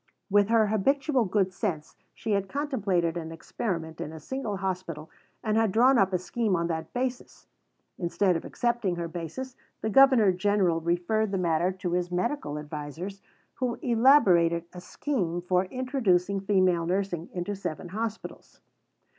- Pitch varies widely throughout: No, average, 4.5 semitones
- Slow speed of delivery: No, average, 155 wpm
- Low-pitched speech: No, high, 190 Hz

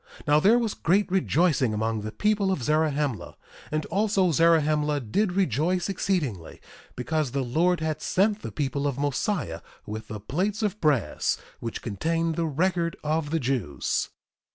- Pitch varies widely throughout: Yes, wide, 5.8 semitones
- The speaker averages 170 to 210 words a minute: No, average, 155 wpm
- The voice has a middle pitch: Yes, medium, 155 Hz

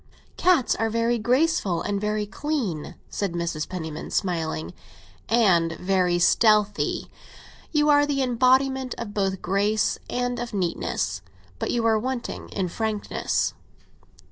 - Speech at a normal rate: No, slow, 125 wpm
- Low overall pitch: No, high, 215 Hz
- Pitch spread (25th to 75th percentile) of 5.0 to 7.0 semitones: Yes, average, 5.3 semitones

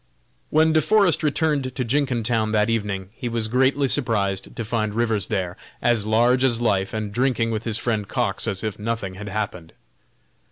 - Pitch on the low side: Yes, low, 115 Hz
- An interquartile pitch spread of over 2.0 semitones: Yes, average, 3.4 semitones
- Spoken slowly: No, average, 175 wpm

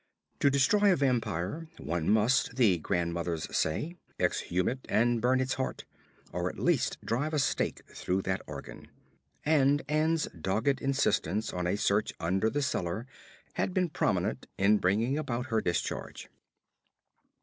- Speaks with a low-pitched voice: Yes, low, 115 Hz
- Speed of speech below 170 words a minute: Yes, average, 145 wpm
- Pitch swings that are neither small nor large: No, wide, 7.3 semitones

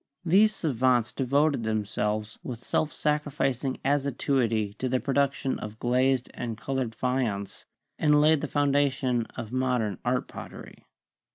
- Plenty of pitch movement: No, average, 3.6 semitones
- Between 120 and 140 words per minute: Yes, slow, 135 wpm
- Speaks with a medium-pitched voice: No, low, 130 Hz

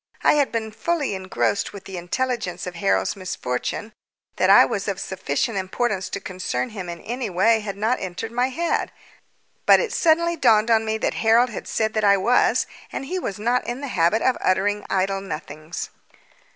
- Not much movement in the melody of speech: No, average, 4.5 semitones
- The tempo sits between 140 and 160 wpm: No, average, 190 wpm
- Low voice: No, high, 215 Hz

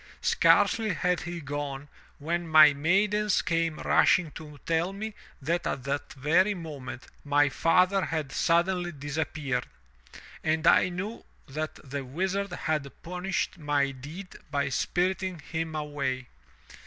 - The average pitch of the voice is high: No, medium, 160 Hz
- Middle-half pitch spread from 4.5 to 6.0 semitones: No, average, 3.9 semitones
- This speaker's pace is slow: Yes, slow, 130 wpm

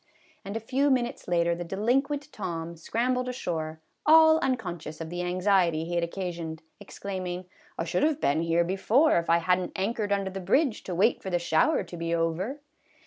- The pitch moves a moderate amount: No, wide, 6.0 semitones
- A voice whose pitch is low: No, medium, 185 Hz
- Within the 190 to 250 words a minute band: Yes, average, 195 wpm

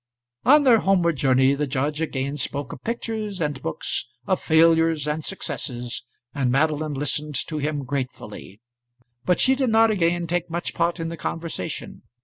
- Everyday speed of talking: Yes, average, 160 wpm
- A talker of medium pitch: Yes, medium, 155 Hz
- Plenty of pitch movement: No, average, 3.8 semitones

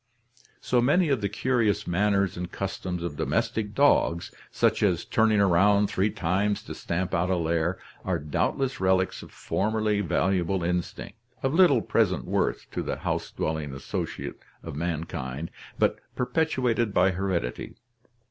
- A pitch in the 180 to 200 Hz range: No, very low, 95 Hz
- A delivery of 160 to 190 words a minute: No, average, 145 wpm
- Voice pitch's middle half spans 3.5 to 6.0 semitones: Yes, average, 4.1 semitones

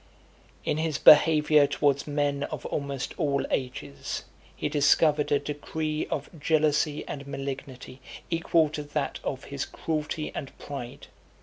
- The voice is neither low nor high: Yes, medium, 145 Hz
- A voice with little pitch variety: Yes, narrow, 1.6 semitones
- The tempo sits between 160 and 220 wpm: No, slow, 135 wpm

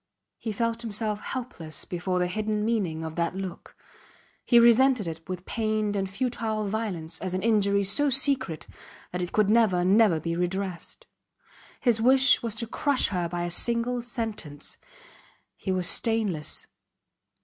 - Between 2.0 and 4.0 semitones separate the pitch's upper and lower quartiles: No, average, 4.4 semitones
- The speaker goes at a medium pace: Yes, average, 150 wpm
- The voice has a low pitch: No, high, 210 Hz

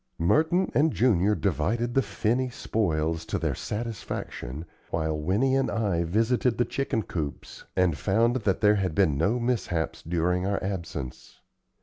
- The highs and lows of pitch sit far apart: Yes, wide, 6.1 semitones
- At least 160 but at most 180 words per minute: No, average, 145 wpm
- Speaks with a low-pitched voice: Yes, low, 100 Hz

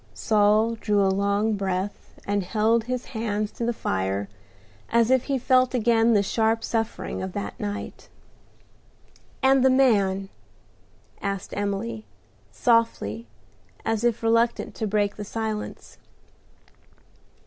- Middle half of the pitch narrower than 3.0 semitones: Yes, narrow, 2.6 semitones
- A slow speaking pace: Yes, slow, 125 wpm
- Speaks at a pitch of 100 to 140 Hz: No, high, 215 Hz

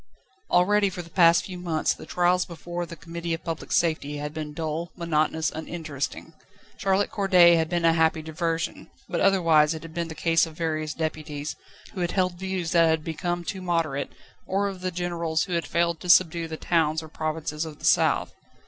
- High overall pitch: No, medium, 165 Hz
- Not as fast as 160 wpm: No, average, 195 wpm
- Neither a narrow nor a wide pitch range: No, narrow, 1.8 semitones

